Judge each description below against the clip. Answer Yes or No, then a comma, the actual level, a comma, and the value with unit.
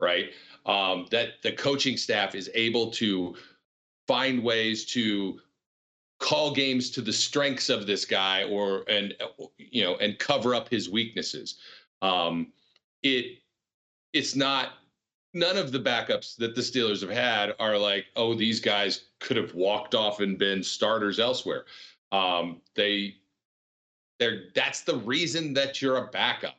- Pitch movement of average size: Yes, average, 4.6 semitones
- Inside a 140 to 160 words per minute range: Yes, average, 145 wpm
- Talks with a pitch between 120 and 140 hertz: No, low, 110 Hz